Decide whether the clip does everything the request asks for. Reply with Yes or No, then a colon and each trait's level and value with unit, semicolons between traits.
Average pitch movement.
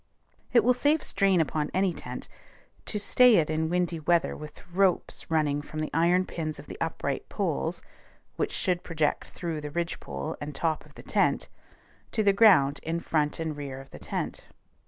Yes: average, 3.7 semitones